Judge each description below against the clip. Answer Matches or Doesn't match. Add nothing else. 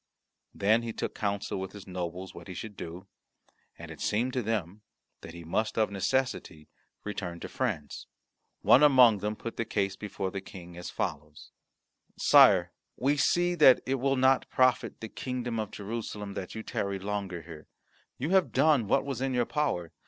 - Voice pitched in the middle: Doesn't match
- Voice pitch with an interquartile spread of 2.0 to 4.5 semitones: Doesn't match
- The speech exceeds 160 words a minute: Matches